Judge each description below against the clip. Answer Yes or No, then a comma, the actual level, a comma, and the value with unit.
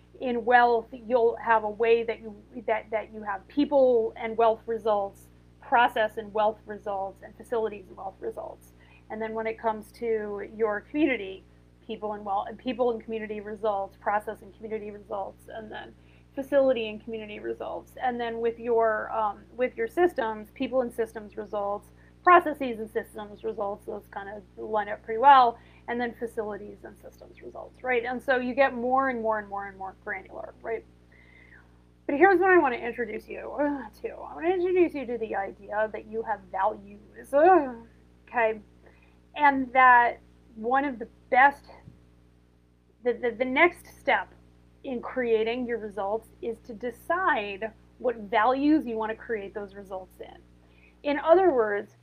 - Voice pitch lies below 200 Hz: No, high, 220 Hz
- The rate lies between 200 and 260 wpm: No, average, 170 wpm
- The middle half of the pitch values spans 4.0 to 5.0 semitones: No, average, 3.4 semitones